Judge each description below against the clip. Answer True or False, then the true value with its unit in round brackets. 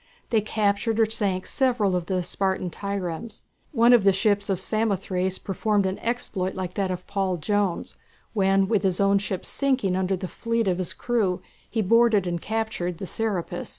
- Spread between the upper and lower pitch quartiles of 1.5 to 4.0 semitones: True (3.0 semitones)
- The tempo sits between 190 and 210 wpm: False (180 wpm)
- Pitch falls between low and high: False (200 Hz)